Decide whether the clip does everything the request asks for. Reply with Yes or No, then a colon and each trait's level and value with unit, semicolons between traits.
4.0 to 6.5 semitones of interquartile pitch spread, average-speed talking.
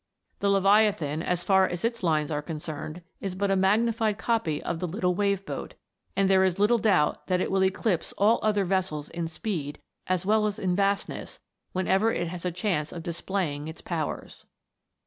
No: average, 3.2 semitones; average, 185 wpm